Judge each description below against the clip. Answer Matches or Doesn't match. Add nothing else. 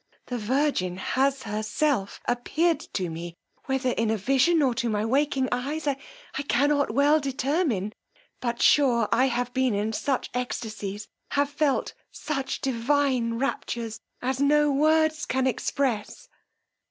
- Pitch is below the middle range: Doesn't match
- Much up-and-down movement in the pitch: Doesn't match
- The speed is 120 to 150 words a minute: Matches